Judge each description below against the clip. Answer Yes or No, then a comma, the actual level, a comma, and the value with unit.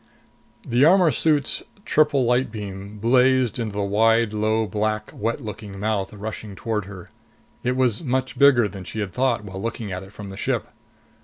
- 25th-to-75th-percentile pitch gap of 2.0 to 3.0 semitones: No, average, 3.6 semitones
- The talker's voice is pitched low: Yes, low, 110 Hz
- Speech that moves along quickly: No, average, 175 wpm